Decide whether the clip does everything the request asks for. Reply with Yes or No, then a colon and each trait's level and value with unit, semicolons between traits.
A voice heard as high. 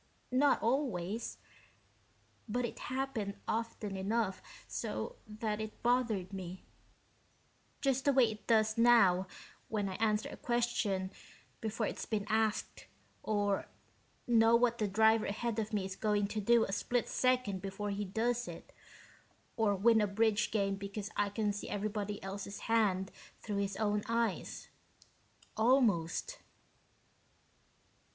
Yes: high, 215 Hz